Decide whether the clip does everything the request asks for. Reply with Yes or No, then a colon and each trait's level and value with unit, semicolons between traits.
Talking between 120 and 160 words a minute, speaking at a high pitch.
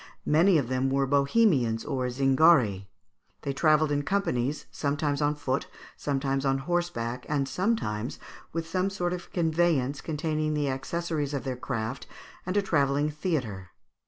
No: average, 150 wpm; medium, 145 Hz